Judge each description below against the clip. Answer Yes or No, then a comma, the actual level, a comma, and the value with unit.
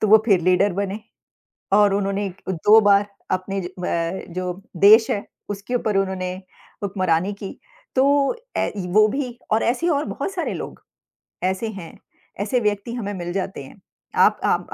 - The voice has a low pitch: No, high, 200 Hz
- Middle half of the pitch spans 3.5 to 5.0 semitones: No, narrow, 2.5 semitones